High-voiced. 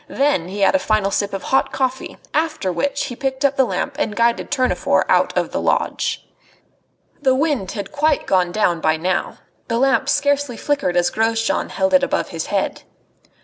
Yes: very high, 255 Hz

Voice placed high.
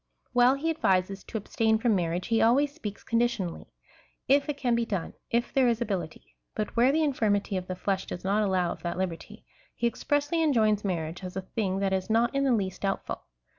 Yes: high, 215 Hz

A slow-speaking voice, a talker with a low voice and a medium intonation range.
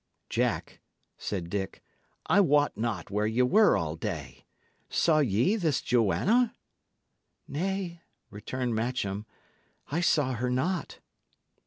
No: slow, 115 wpm; low, 125 Hz; wide, 8.4 semitones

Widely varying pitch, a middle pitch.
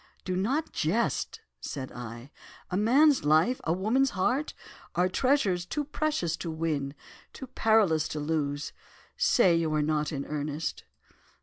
Yes: wide, 7.6 semitones; medium, 170 Hz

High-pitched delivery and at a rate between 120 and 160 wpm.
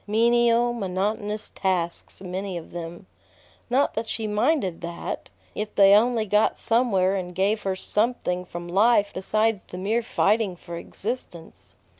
Yes: high, 205 Hz; average, 140 wpm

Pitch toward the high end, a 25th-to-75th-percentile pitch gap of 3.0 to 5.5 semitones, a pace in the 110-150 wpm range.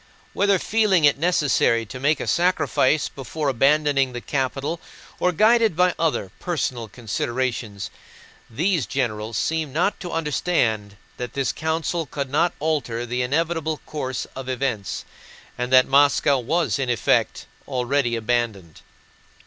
No: medium, 140 Hz; average, 4.8 semitones; slow, 135 wpm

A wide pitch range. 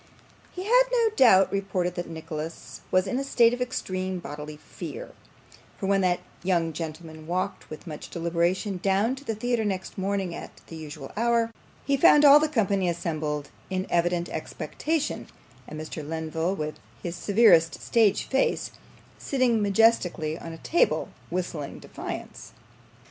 Yes: wide, 5.7 semitones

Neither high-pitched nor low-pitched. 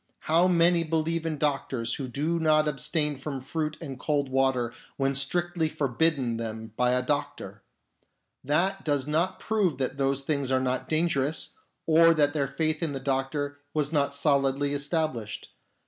Yes: medium, 145 Hz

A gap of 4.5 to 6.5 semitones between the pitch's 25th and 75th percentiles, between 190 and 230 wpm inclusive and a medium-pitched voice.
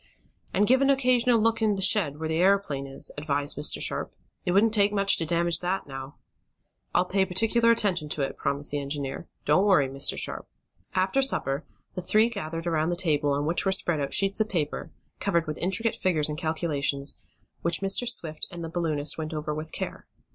Yes: average, 5.0 semitones; average, 200 wpm; medium, 170 Hz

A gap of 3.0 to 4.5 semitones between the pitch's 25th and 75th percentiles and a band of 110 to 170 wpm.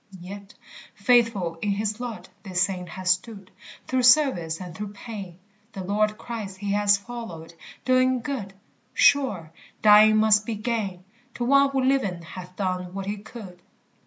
Yes: average, 4.1 semitones; average, 155 wpm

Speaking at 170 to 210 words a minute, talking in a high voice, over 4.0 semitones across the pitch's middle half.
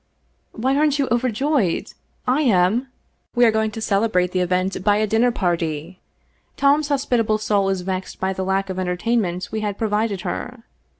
Yes: average, 180 wpm; high, 210 Hz; average, 4.4 semitones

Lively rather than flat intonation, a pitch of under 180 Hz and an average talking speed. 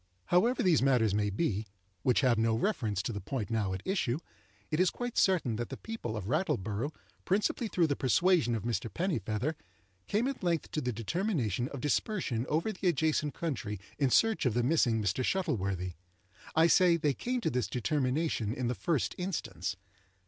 Yes: wide, 7.8 semitones; low, 135 Hz; average, 180 wpm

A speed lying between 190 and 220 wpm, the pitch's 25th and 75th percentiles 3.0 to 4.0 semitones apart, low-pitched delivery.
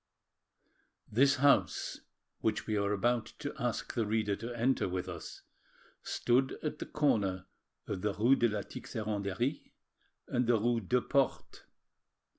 No: average, 140 wpm; average, 3.6 semitones; low, 115 Hz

